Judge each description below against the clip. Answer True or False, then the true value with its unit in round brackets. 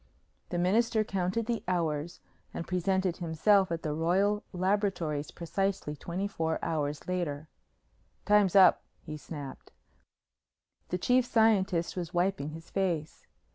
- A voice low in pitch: False (180 Hz)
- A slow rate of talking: True (125 wpm)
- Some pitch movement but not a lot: True (3.5 semitones)